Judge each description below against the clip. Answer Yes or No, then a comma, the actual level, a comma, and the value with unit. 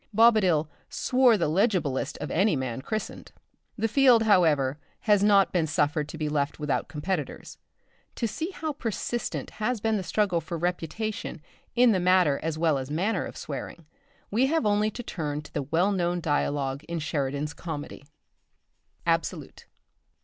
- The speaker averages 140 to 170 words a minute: Yes, average, 155 wpm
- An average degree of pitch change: No, wide, 6.3 semitones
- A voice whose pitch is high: No, medium, 175 Hz